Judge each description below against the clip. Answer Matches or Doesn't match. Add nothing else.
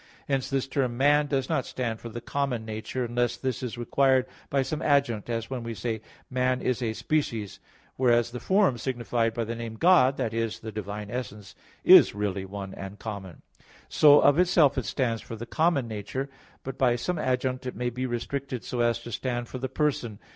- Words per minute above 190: Matches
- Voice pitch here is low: Matches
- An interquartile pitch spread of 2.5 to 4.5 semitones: Matches